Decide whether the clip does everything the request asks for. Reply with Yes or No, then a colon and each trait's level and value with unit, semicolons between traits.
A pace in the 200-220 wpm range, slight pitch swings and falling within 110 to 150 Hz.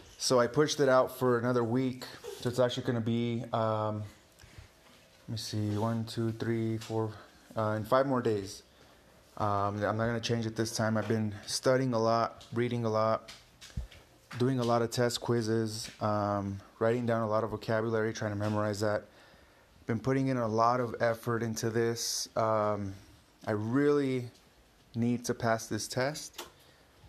No: average, 175 wpm; narrow, 2.1 semitones; low, 115 Hz